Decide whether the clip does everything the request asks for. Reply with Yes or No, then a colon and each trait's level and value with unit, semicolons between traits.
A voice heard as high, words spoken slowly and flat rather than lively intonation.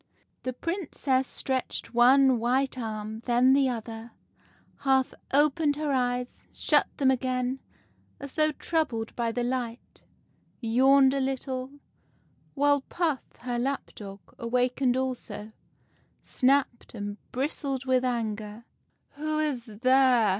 Yes: very high, 255 Hz; slow, 125 wpm; narrow, 2.3 semitones